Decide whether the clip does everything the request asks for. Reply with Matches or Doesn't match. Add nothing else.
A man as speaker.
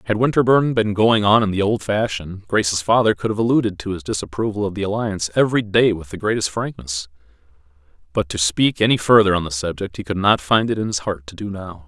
Matches